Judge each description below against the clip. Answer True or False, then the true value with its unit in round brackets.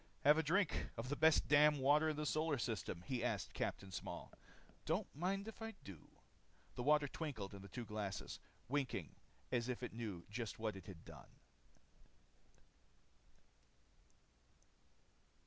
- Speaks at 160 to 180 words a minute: False (145 wpm)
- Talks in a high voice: False (130 Hz)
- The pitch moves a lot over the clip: True (6.1 semitones)